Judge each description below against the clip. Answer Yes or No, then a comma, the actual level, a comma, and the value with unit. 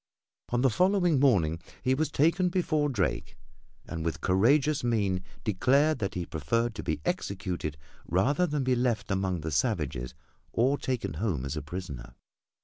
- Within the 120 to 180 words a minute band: Yes, average, 155 wpm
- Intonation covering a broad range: Yes, wide, 8.4 semitones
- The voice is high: No, low, 115 Hz